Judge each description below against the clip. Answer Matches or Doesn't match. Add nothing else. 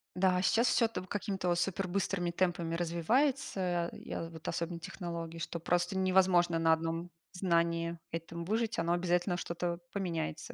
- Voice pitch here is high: Doesn't match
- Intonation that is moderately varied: Doesn't match